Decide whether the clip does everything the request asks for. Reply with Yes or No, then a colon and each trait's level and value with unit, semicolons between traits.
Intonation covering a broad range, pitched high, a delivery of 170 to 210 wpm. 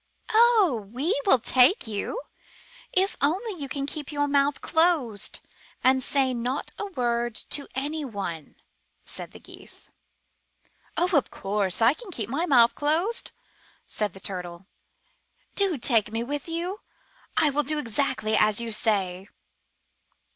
No: wide, 6.1 semitones; very high, 265 Hz; average, 140 wpm